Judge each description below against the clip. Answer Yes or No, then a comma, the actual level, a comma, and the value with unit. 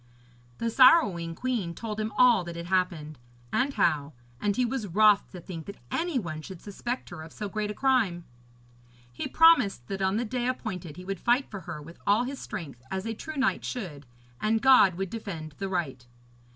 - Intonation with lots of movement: Yes, wide, 6.0 semitones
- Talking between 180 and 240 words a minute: Yes, average, 200 wpm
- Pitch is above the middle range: Yes, high, 200 Hz